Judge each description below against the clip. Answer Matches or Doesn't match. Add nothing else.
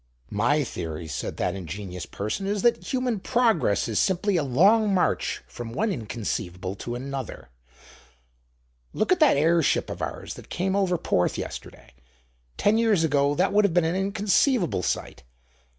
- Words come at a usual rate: Matches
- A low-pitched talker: Doesn't match